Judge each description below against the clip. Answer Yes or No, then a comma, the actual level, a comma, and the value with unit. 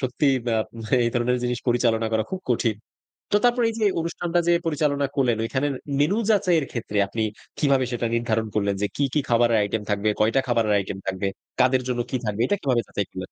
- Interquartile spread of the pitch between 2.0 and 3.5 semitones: No, average, 4.3 semitones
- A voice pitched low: Yes, low, 120 Hz